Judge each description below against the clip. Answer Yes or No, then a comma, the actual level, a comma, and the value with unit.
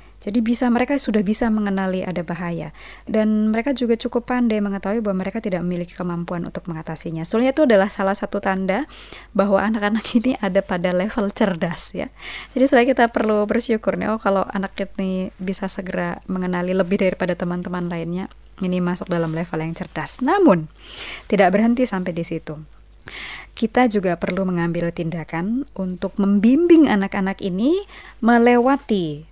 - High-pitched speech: Yes, high, 195 Hz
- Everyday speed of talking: No, fast, 150 wpm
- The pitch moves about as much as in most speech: Yes, average, 4.0 semitones